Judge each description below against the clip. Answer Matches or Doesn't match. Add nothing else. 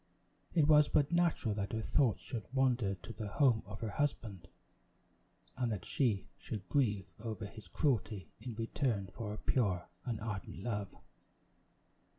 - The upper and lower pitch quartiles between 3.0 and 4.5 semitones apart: Matches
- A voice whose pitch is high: Doesn't match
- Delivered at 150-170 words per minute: Matches